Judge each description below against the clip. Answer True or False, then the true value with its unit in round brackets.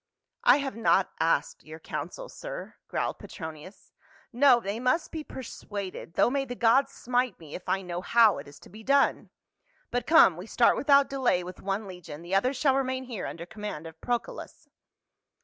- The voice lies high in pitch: True (225 Hz)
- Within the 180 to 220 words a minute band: True (185 wpm)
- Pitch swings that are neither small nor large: False (6.8 semitones)